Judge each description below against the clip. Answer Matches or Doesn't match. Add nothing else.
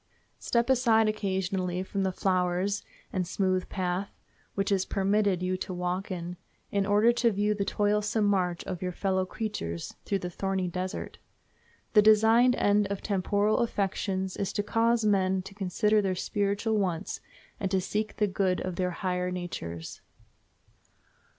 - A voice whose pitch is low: Doesn't match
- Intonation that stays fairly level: Matches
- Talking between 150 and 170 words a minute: Matches